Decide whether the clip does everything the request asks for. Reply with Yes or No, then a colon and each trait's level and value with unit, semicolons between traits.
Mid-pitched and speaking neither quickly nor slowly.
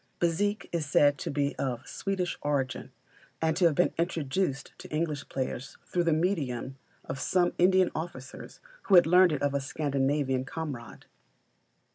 Yes: medium, 150 Hz; average, 155 wpm